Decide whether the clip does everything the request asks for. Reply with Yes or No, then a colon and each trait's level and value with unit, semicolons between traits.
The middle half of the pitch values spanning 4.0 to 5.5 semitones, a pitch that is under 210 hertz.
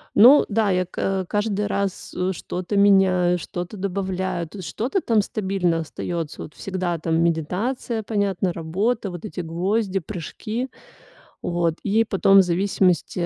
No: average, 2.7 semitones; high, 190 Hz